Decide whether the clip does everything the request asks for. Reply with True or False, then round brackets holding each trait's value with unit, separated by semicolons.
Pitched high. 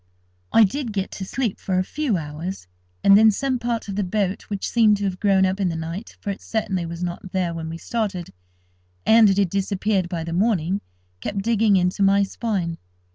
True (195 Hz)